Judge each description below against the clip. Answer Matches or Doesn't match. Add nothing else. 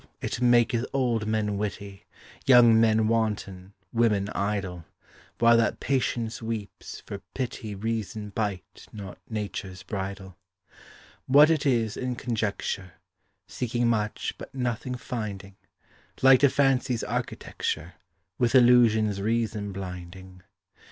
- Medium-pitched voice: Doesn't match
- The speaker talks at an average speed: Doesn't match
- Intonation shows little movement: Doesn't match